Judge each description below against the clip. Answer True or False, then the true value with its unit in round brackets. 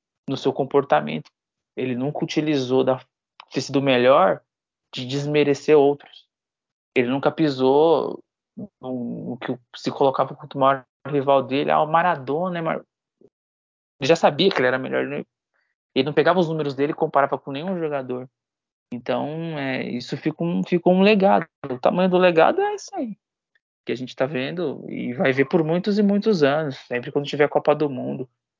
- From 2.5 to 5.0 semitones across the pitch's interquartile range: True (3.9 semitones)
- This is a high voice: False (140 Hz)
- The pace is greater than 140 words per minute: True (165 wpm)